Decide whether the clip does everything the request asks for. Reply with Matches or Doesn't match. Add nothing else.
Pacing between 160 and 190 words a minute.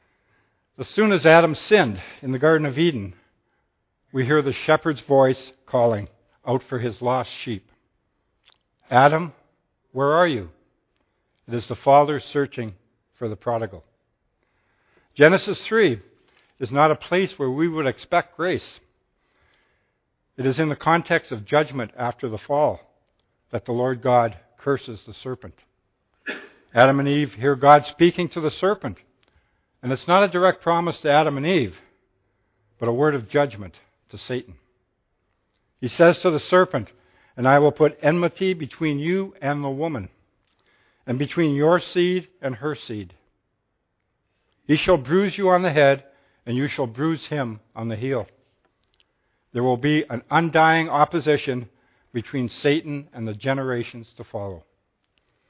Doesn't match